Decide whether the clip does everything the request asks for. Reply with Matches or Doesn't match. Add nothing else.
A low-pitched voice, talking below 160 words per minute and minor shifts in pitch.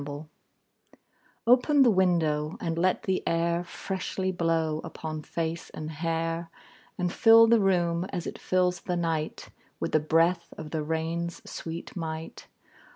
Doesn't match